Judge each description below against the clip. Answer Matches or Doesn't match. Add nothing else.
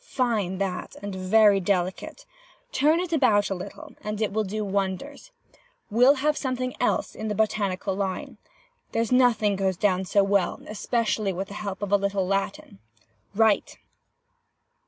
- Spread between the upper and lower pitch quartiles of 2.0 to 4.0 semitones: Matches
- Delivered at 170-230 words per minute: Doesn't match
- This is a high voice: Matches